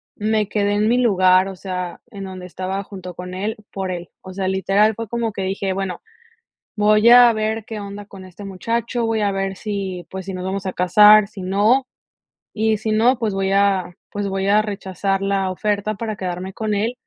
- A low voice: No, high, 200 Hz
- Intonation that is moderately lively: No, narrow, 2.1 semitones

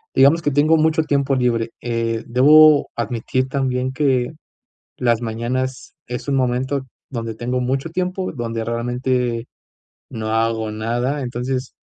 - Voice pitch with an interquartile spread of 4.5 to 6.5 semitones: No, average, 2.9 semitones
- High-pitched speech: No, low, 125 Hz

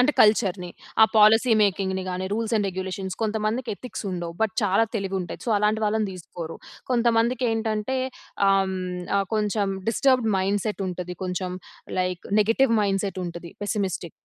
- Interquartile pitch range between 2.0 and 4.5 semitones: Yes, average, 3.1 semitones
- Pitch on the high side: Yes, high, 205 Hz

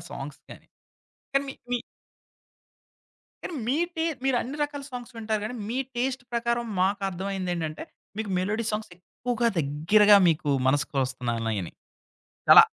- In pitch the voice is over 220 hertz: No, high, 210 Hz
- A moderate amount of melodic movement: No, wide, 7.0 semitones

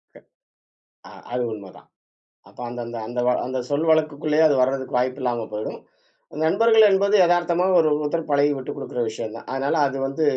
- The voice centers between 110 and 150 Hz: Yes, medium, 140 Hz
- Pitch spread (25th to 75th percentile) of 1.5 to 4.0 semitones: No, average, 4.5 semitones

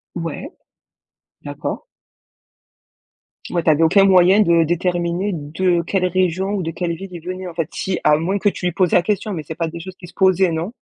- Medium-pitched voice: Yes, medium, 175 Hz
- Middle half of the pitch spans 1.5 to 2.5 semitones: Yes, narrow, 2.2 semitones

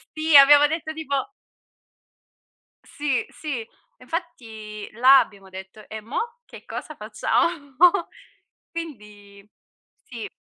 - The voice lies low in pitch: No, very high, 265 Hz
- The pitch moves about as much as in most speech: No, wide, 6.6 semitones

